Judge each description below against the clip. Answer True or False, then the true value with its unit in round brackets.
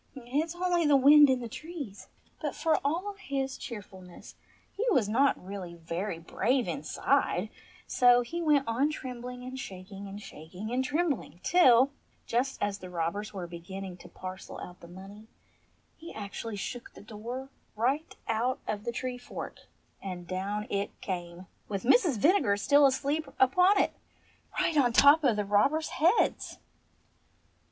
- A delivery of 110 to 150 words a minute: False (160 wpm)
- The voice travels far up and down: True (6.1 semitones)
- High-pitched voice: True (240 Hz)